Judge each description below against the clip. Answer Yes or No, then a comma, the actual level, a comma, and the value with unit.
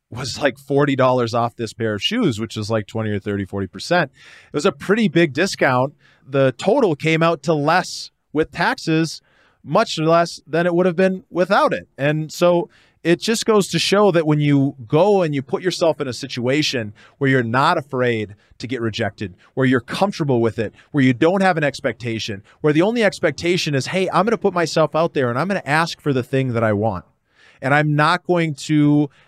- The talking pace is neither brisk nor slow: No, fast, 210 wpm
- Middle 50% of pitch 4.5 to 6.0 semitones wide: Yes, wide, 5.4 semitones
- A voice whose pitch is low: No, medium, 145 Hz